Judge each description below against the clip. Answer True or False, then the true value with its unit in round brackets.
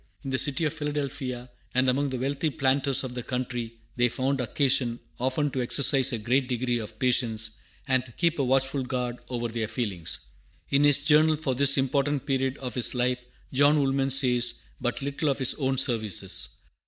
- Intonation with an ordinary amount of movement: False (2.2 semitones)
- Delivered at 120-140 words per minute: False (185 wpm)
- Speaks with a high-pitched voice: False (130 Hz)